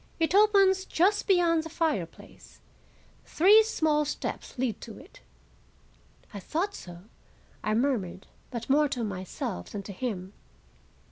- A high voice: Yes, very high, 295 Hz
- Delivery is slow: Yes, slow, 130 wpm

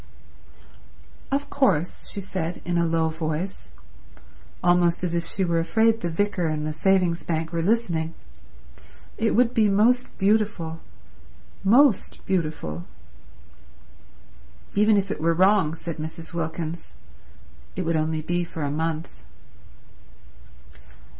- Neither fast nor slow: No, slow, 120 wpm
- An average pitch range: Yes, average, 3.8 semitones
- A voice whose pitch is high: No, medium, 170 Hz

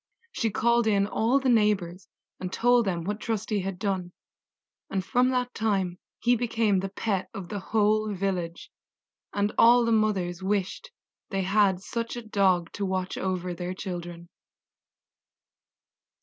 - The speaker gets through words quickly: No, average, 150 wpm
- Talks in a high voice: Yes, high, 200 Hz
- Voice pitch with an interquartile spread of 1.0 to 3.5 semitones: Yes, average, 3.2 semitones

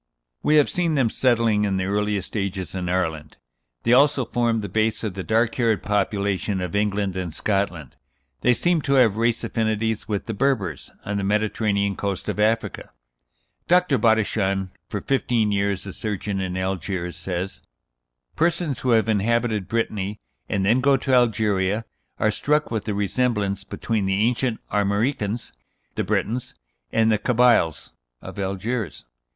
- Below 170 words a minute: Yes, average, 155 wpm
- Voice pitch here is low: Yes, low, 105 Hz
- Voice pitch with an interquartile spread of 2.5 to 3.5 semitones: Yes, average, 3.2 semitones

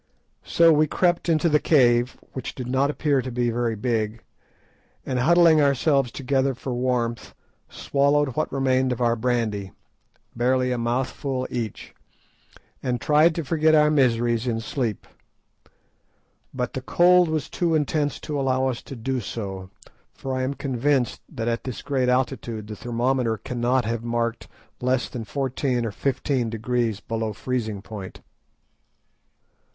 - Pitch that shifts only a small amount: No, average, 3.0 semitones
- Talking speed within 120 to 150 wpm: Yes, average, 145 wpm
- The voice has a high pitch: No, low, 125 Hz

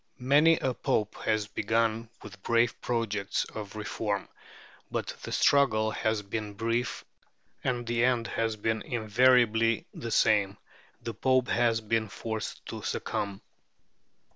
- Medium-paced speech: No, slow, 130 wpm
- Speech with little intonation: Yes, narrow, 1.9 semitones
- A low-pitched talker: Yes, low, 110 Hz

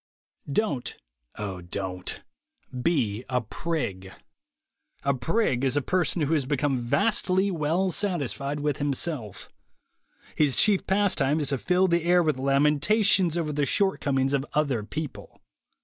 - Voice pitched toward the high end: No, medium, 145 Hz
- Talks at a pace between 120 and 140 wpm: Yes, slow, 135 wpm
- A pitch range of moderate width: Yes, average, 4.9 semitones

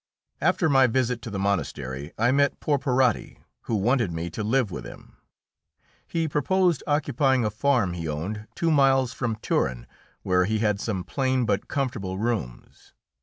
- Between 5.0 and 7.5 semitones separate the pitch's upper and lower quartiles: Yes, wide, 5.6 semitones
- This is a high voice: No, low, 115 Hz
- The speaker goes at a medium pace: Yes, average, 160 wpm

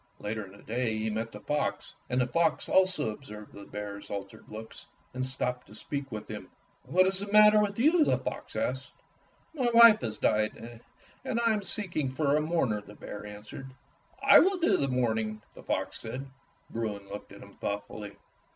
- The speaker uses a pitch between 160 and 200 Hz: No, low, 125 Hz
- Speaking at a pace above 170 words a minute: Yes, average, 190 wpm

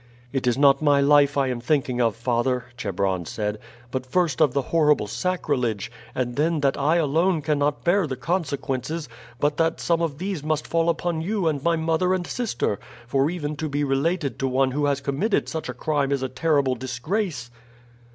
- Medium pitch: Yes, medium, 145 Hz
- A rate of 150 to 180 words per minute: No, average, 190 wpm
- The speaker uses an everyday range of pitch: Yes, average, 4.1 semitones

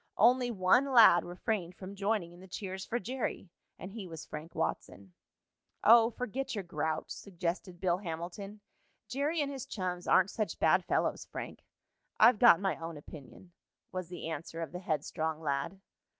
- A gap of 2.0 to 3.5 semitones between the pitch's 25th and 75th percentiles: No, average, 4.6 semitones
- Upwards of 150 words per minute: Yes, average, 165 wpm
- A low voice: No, medium, 185 Hz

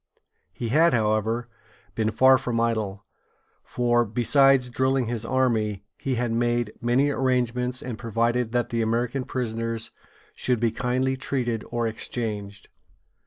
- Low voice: Yes, low, 120 Hz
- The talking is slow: Yes, slow, 130 wpm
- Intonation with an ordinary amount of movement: No, narrow, 2.1 semitones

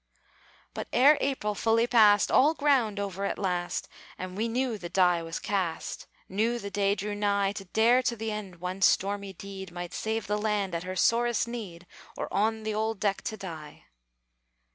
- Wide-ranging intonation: No, average, 2.9 semitones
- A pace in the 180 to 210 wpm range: Yes, average, 185 wpm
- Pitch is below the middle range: No, high, 205 Hz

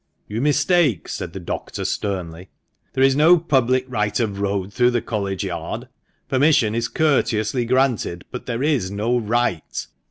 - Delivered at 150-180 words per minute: Yes, average, 155 wpm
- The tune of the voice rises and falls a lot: No, average, 4.7 semitones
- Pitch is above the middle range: No, low, 120 Hz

